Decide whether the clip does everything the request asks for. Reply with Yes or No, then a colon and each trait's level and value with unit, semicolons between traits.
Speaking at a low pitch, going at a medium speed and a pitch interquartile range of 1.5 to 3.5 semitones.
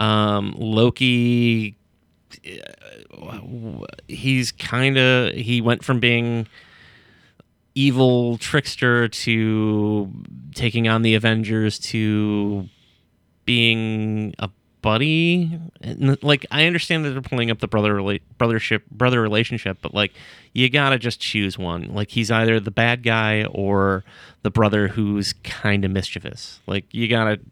No: low, 110 Hz; slow, 125 wpm; average, 2.7 semitones